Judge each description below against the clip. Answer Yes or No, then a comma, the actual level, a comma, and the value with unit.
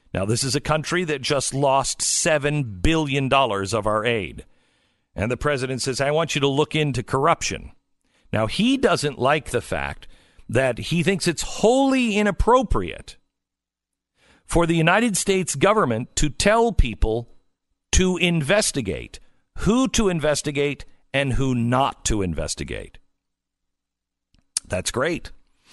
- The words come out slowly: Yes, slow, 130 wpm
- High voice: No, medium, 140 Hz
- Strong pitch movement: Yes, wide, 7.6 semitones